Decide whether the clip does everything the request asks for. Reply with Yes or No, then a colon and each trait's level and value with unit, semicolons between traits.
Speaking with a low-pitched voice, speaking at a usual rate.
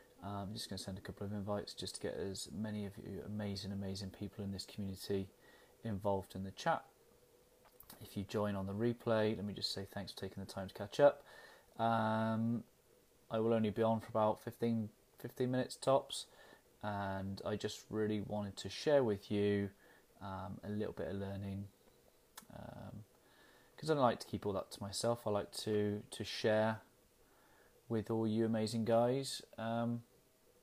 Yes: low, 105 Hz; average, 185 wpm